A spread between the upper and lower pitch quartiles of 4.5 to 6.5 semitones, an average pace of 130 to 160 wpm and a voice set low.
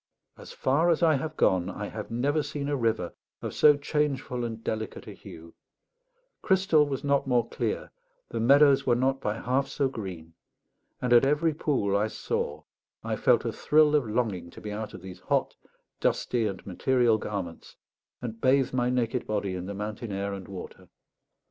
No: wide, 5.6 semitones; average, 180 wpm; low, 120 Hz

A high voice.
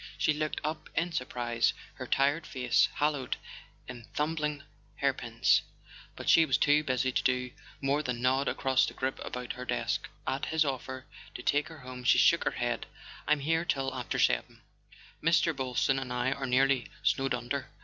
No: low, 135 Hz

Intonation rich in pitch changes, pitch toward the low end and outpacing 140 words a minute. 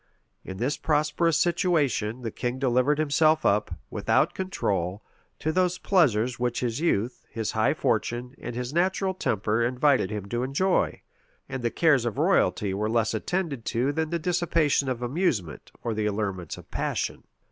Yes: wide, 6.0 semitones; low, 125 Hz; average, 160 wpm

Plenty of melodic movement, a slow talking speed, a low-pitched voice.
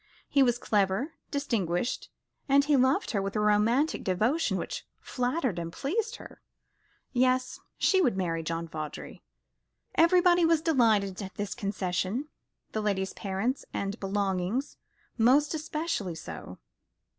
No: wide, 6.8 semitones; slow, 130 wpm; high, 225 Hz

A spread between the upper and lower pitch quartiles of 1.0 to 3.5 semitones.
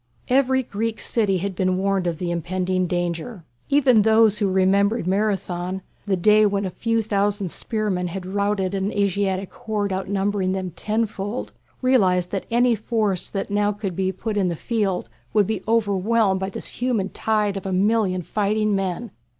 Yes: narrow, 2.5 semitones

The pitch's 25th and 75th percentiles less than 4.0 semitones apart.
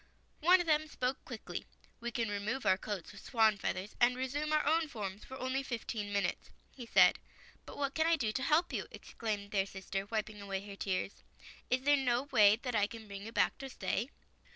No: average, 5.0 semitones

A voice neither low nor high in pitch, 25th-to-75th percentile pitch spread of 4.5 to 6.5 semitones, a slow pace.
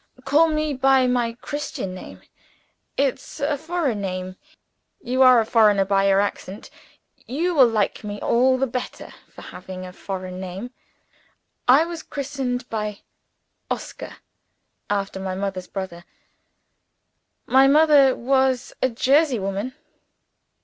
No: high, 245 Hz; wide, 5.6 semitones; slow, 125 wpm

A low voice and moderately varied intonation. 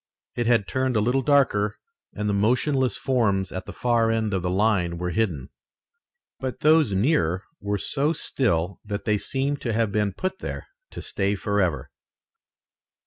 Yes: low, 105 Hz; average, 4.8 semitones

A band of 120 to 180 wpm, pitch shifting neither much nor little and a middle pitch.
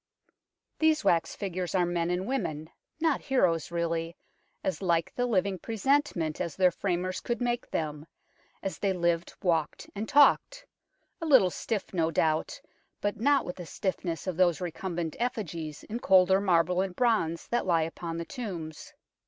Yes: average, 160 wpm; average, 4.6 semitones; medium, 180 Hz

